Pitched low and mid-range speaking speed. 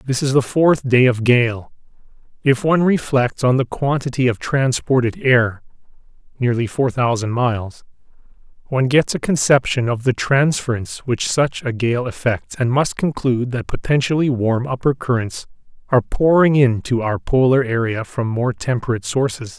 Yes: low, 125 Hz; average, 155 wpm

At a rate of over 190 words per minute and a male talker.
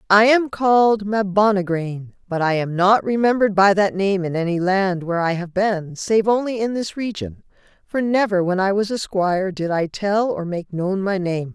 No: fast, 205 wpm; female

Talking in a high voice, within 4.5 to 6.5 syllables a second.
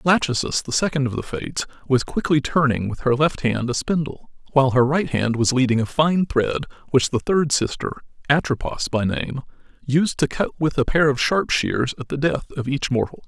No: low, 135 Hz; 5.2 syllables/s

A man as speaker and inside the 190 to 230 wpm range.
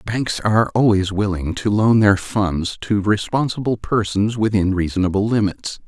No: male; average, 145 wpm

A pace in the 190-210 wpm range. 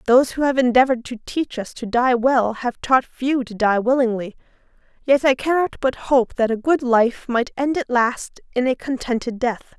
Yes: average, 200 wpm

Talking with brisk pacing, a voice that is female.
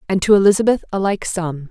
Yes: fast, 210 wpm; female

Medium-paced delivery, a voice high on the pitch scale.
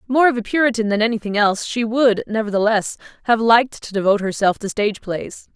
Yes: average, 195 wpm; high, 220 Hz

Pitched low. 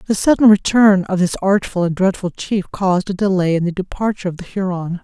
No: high, 190 Hz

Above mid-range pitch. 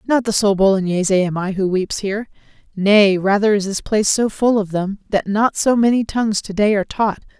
Yes: high, 205 Hz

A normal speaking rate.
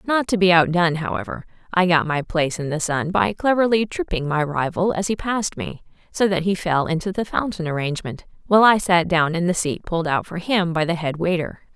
No: fast, 225 wpm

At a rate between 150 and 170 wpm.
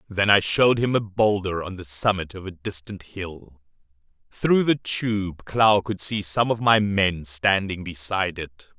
No: average, 180 wpm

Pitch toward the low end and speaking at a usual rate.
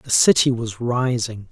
Yes: low, 120 Hz; average, 160 wpm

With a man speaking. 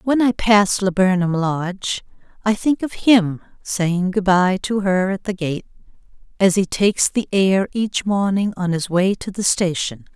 No: female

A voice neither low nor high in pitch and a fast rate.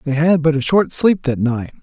Yes: medium, 150 Hz; fast, 260 wpm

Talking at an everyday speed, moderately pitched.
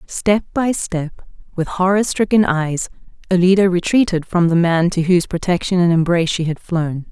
Yes: average, 170 wpm; medium, 175 Hz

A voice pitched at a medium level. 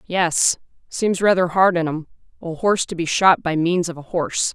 Yes: medium, 175 Hz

